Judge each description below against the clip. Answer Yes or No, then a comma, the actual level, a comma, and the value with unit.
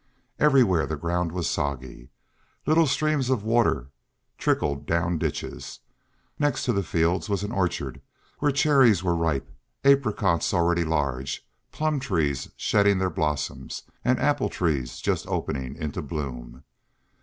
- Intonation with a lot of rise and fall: Yes, wide, 8.2 semitones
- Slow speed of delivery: Yes, slow, 130 wpm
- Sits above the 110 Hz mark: No, very low, 85 Hz